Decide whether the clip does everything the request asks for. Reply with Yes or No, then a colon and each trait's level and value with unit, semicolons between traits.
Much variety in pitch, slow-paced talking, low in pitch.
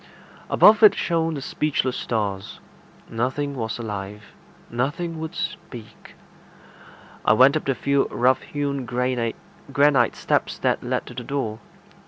No: average, 3.9 semitones; slow, 130 wpm; low, 130 Hz